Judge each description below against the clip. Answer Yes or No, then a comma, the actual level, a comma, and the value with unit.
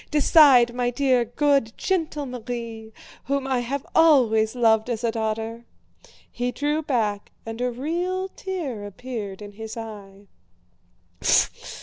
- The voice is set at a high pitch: Yes, high, 245 Hz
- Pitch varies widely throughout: No, average, 4.1 semitones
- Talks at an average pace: No, slow, 125 wpm